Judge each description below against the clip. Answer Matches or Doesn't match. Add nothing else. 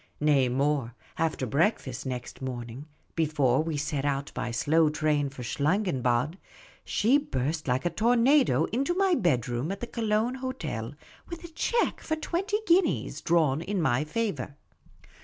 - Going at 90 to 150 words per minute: Matches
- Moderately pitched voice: Matches